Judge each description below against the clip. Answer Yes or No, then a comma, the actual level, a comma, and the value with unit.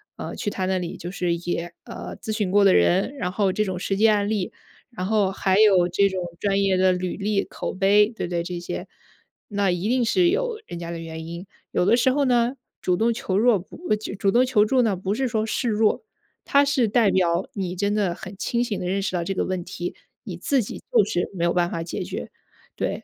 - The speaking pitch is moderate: No, high, 195 Hz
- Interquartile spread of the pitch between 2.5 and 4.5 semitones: Yes, average, 3.6 semitones